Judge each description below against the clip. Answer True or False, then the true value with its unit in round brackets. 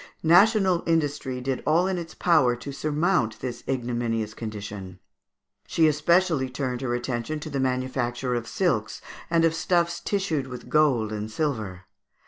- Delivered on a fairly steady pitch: False (5.4 semitones)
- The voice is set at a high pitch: False (130 Hz)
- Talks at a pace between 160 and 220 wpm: False (145 wpm)